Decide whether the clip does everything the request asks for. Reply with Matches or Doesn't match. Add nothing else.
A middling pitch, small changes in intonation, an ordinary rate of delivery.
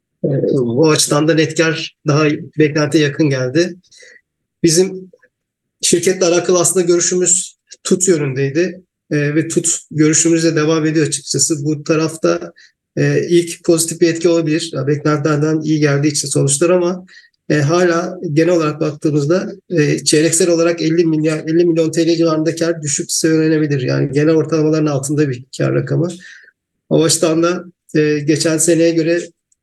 Doesn't match